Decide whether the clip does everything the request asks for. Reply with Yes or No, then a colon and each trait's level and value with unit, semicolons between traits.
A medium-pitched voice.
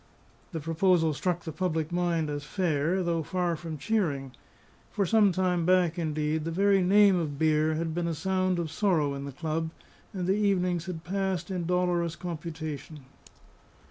Yes: medium, 170 Hz